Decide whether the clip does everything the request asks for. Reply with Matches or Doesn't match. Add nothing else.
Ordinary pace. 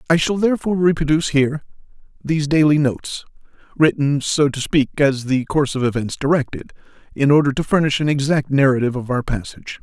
Matches